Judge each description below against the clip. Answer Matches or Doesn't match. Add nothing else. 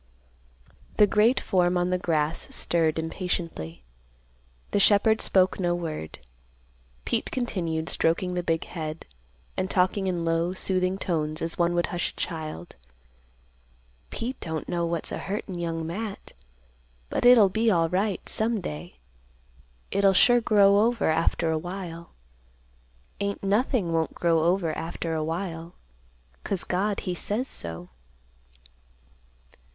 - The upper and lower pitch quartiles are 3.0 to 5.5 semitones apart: Matches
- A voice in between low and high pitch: Matches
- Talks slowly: Matches